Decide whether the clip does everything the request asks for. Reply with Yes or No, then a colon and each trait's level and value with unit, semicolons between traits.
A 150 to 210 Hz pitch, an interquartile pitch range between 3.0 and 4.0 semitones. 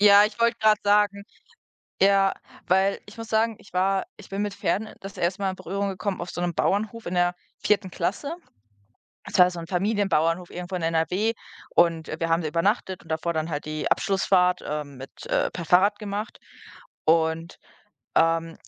Yes: medium, 185 Hz; average, 3.4 semitones